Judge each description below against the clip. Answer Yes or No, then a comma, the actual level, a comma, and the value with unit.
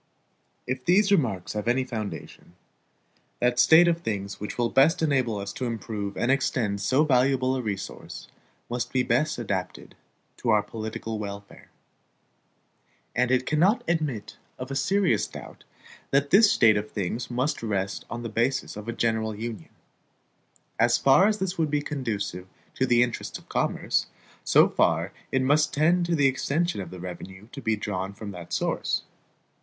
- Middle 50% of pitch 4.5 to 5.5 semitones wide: Yes, average, 5.0 semitones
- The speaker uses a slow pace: No, average, 165 wpm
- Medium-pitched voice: No, low, 120 Hz